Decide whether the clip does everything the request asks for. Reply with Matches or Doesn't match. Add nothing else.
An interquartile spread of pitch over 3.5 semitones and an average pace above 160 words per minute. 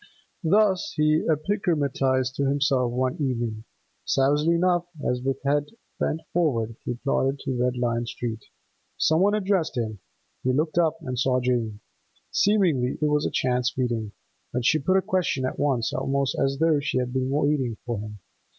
Matches